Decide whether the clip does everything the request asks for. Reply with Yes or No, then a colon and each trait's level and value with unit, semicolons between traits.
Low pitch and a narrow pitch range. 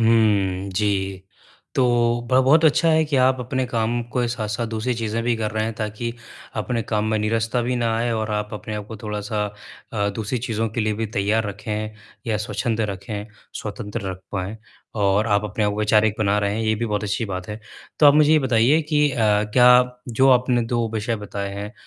Yes: low, 110 Hz; narrow, 2.3 semitones